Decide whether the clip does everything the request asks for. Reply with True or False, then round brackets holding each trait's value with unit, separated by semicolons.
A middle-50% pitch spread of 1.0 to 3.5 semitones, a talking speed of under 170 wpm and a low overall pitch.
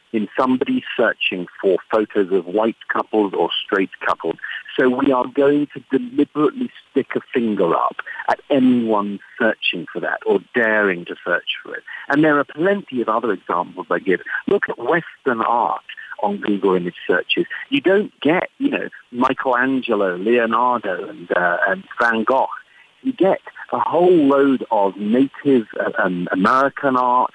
False (4.1 semitones; 160 wpm; 130 Hz)